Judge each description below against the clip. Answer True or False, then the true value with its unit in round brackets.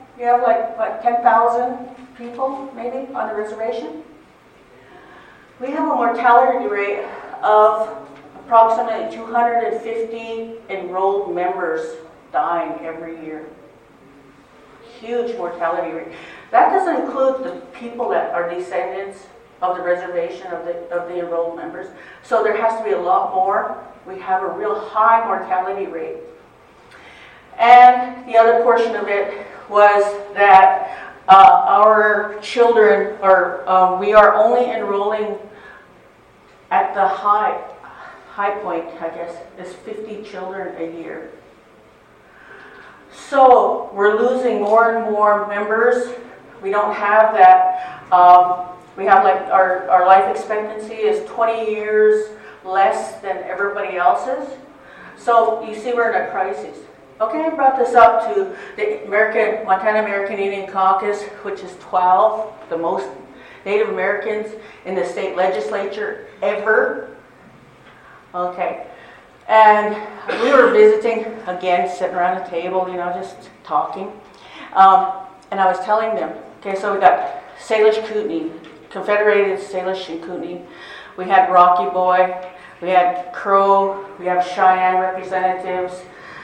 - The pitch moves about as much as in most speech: True (3.9 semitones)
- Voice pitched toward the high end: True (205 Hz)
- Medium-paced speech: False (130 wpm)